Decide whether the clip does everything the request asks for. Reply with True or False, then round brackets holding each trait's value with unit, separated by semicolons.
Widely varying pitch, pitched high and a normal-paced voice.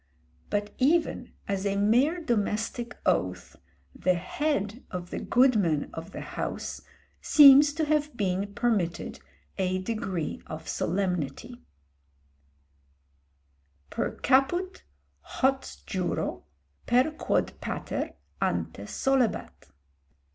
False (6.5 semitones; 215 Hz; 95 wpm)